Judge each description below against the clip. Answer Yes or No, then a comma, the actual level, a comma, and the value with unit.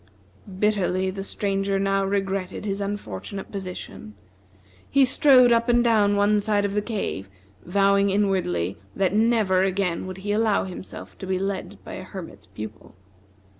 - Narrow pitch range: Yes, narrow, 1.8 semitones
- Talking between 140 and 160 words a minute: Yes, average, 150 wpm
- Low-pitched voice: No, high, 195 Hz